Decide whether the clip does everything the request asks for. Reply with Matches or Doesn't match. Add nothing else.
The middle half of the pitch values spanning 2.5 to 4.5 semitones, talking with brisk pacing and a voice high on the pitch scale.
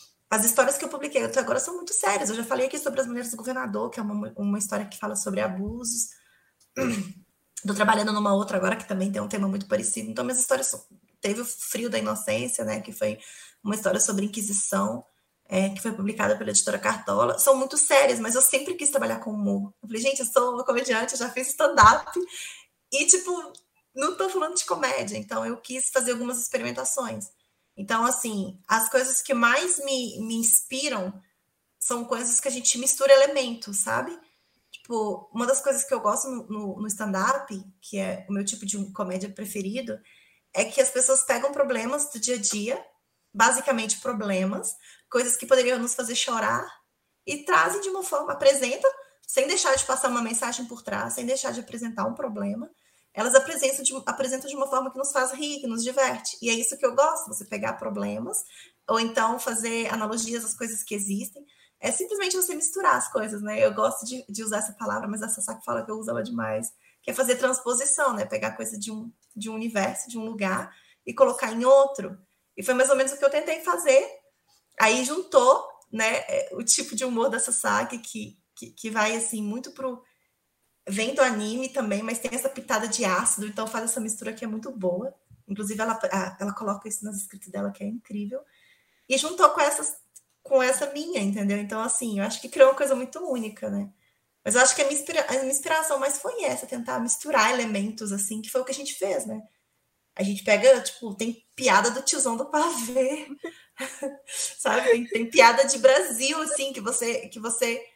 Matches